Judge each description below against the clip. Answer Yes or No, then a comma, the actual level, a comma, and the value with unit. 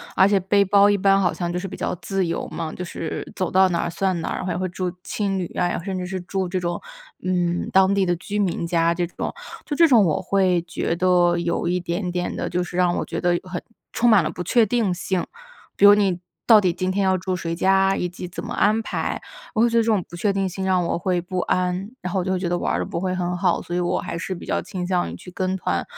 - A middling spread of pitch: No, narrow, 1.8 semitones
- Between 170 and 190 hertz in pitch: Yes, medium, 185 Hz